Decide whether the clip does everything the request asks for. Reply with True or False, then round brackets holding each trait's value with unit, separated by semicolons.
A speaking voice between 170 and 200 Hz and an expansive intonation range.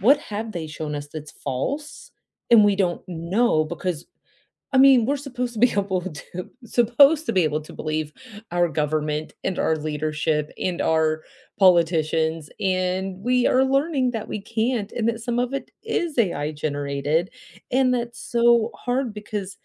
True (190 Hz; 7.4 semitones)